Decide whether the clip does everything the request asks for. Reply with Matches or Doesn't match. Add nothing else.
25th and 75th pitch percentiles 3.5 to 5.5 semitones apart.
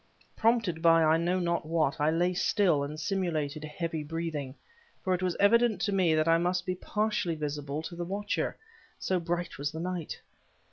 Doesn't match